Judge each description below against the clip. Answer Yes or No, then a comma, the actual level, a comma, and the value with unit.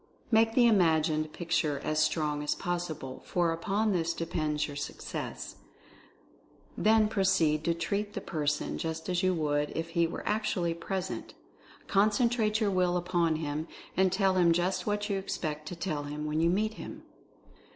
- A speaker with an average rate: Yes, average, 160 wpm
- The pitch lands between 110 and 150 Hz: No, medium, 170 Hz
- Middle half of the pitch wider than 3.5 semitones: Yes, average, 4.0 semitones